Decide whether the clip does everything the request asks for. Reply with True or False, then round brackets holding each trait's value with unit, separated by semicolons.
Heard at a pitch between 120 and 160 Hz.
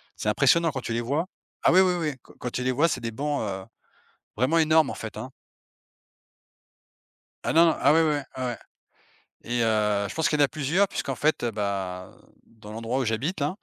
True (135 Hz)